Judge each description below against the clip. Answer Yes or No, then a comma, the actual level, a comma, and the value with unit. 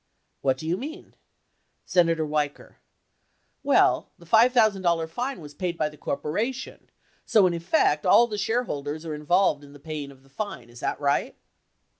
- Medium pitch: Yes, medium, 165 Hz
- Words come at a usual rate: Yes, average, 155 wpm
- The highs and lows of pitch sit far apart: Yes, wide, 6.3 semitones